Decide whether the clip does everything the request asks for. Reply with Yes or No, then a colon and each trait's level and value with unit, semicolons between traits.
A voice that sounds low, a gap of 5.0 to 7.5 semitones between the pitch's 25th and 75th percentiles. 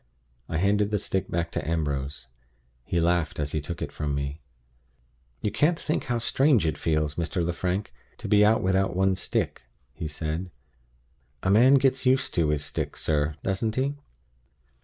Yes: very low, 90 Hz; average, 5.3 semitones